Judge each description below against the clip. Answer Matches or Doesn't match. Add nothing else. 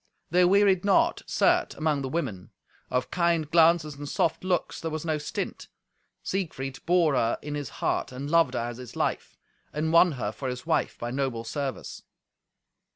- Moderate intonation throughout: Matches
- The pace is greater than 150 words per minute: Matches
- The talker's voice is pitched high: Doesn't match